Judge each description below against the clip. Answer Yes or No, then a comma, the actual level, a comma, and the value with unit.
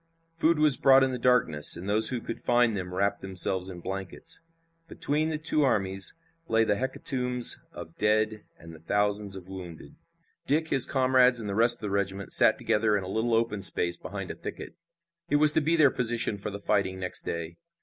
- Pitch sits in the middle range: No, low, 105 Hz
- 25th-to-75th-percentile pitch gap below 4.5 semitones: No, average, 4.9 semitones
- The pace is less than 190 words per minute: No, average, 200 wpm